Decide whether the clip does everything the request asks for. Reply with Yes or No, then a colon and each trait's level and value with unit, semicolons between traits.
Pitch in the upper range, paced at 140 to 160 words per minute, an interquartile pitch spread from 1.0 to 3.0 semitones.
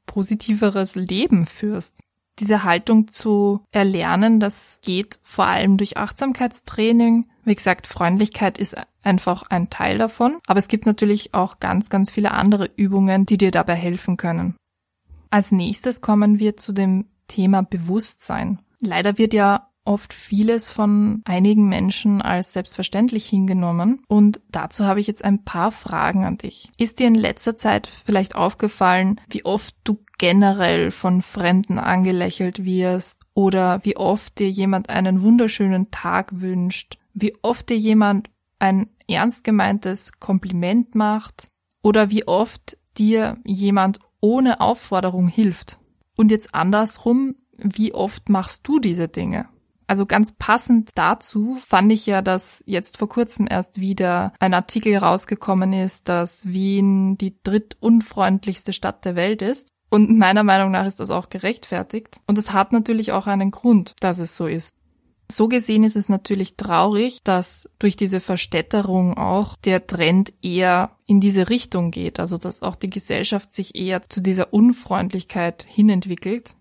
Yes: high, 200 Hz; average, 145 wpm; narrow, 2.4 semitones